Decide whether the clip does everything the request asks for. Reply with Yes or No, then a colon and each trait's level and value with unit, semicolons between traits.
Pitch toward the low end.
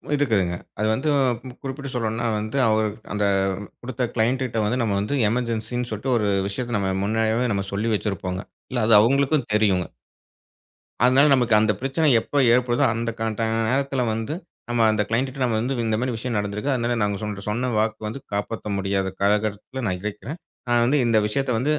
Yes: low, 115 Hz